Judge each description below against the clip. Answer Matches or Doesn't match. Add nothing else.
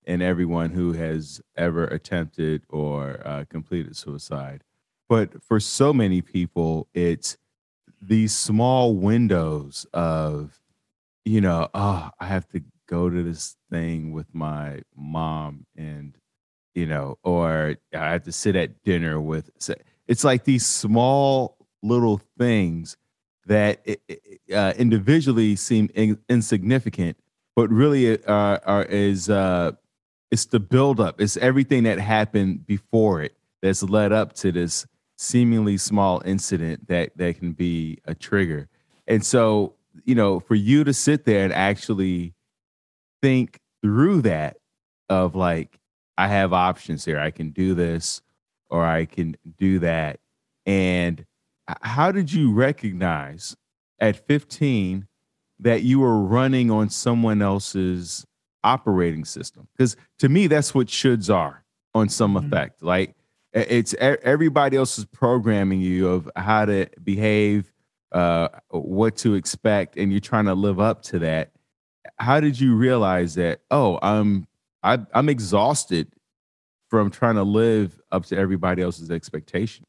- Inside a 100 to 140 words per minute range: Matches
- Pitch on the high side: Doesn't match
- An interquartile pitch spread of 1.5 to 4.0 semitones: Doesn't match